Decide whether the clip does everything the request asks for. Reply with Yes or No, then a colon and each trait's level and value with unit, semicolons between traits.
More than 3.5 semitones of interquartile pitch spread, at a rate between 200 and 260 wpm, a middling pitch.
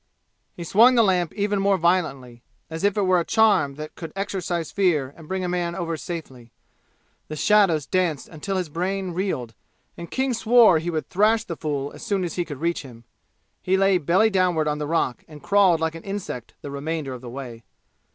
Yes: average, 4.3 semitones; fast, 205 wpm; medium, 170 Hz